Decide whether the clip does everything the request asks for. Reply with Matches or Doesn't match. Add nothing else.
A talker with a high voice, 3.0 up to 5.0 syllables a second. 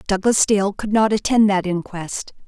Matches